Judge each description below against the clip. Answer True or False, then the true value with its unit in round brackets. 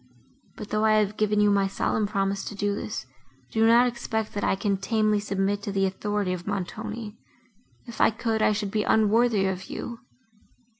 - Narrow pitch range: True (1.8 semitones)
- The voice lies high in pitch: True (210 Hz)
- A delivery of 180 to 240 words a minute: True (190 wpm)